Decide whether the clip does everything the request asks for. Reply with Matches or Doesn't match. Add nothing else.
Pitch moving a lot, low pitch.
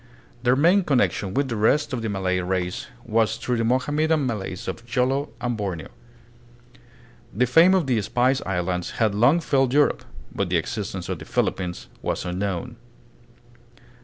Matches